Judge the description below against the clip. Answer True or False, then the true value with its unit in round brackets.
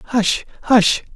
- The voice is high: True (220 Hz)